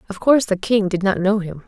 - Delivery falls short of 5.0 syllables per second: No, 6.1 syllables/s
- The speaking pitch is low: No, high, 200 Hz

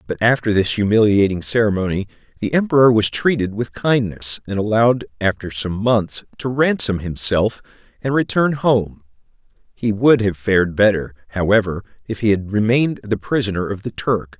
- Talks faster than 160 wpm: No, average, 155 wpm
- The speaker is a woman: No, male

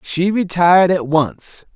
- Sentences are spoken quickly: No, slow, 135 wpm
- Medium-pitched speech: Yes, medium, 170 Hz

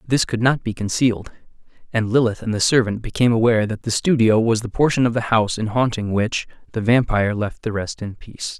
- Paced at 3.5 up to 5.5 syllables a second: No, 6.0 syllables/s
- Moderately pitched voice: No, low, 115 Hz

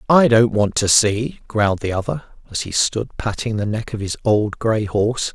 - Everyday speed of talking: No, fast, 215 wpm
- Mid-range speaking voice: No, low, 110 Hz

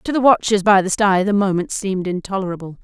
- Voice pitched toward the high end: Yes, high, 195 Hz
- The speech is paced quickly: Yes, fast, 210 wpm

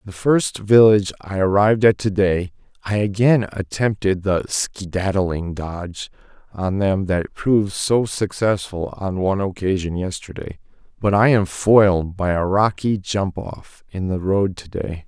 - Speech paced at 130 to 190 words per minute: Yes, average, 150 wpm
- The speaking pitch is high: No, very low, 95 Hz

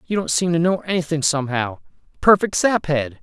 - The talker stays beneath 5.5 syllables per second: No, 5.7 syllables/s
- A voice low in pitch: No, medium, 160 Hz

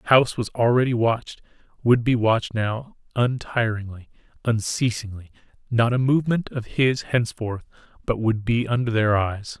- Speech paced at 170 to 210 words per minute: No, average, 145 wpm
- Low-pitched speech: Yes, low, 115 Hz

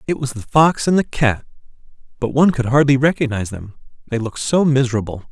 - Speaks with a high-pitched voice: No, low, 130 Hz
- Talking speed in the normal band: Yes, average, 190 wpm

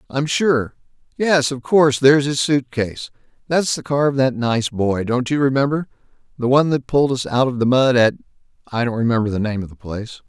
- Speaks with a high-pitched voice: No, low, 130 Hz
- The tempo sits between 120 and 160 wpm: No, average, 180 wpm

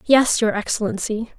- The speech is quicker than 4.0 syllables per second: Yes, 4.7 syllables/s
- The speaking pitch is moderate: No, high, 225 Hz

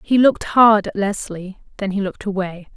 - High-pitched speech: Yes, high, 200 Hz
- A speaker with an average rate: Yes, average, 195 wpm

